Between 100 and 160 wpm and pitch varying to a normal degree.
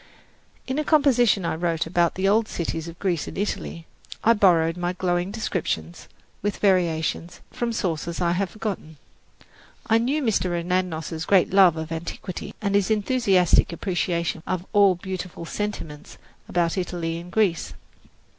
Yes: average, 150 wpm; average, 3.3 semitones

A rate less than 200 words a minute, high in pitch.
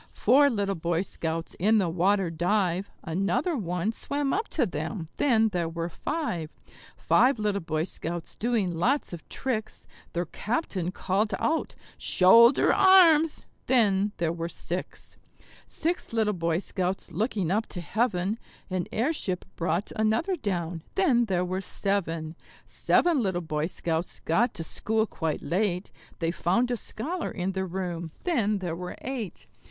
Yes: average, 145 wpm; high, 195 Hz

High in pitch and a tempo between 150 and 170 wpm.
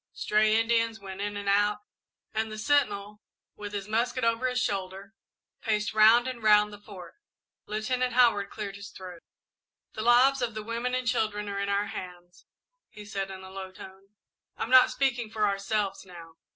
No: high, 210 Hz; average, 180 wpm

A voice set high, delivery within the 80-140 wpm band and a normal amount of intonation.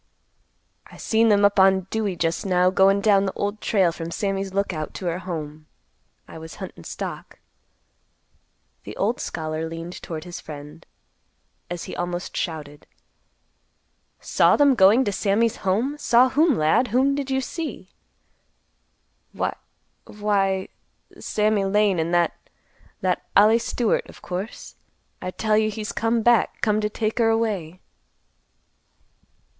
Yes: high, 195 Hz; slow, 135 wpm; average, 4.1 semitones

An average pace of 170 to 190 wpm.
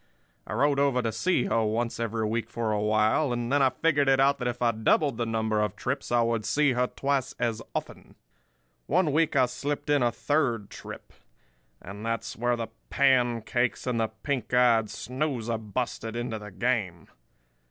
Yes: average, 185 wpm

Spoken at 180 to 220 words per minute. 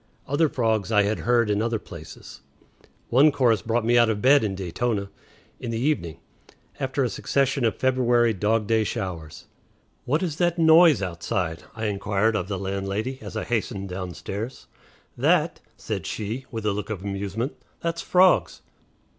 No: average, 165 wpm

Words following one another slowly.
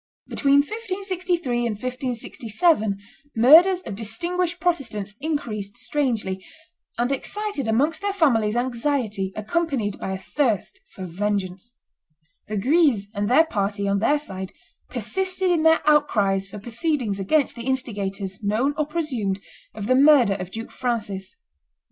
Yes: slow, 130 wpm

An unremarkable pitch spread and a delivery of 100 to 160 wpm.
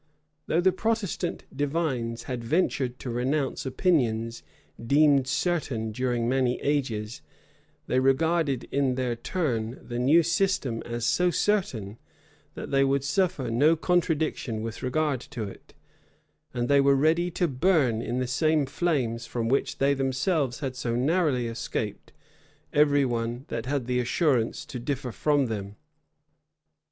Yes: average, 4.5 semitones; average, 140 wpm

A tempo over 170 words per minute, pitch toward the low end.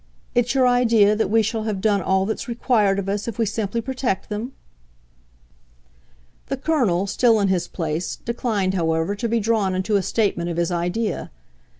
No: average, 180 wpm; high, 210 Hz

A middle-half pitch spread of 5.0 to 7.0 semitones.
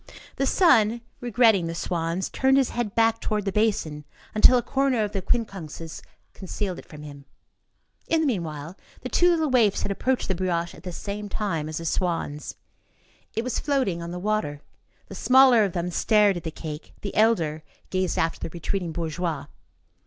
Yes: wide, 5.5 semitones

